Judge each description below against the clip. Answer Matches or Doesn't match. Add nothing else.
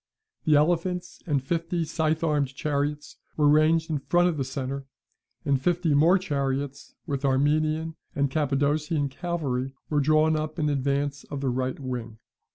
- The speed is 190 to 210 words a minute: Doesn't match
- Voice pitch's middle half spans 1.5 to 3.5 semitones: Matches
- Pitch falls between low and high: Matches